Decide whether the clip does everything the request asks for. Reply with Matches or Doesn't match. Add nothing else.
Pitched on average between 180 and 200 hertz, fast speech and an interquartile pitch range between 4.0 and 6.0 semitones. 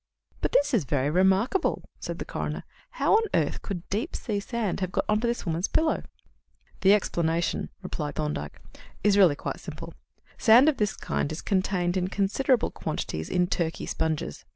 Doesn't match